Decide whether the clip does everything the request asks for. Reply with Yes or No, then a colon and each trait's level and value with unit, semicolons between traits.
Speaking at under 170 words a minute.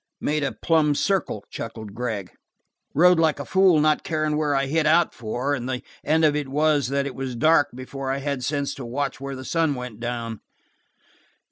No: average, 200 wpm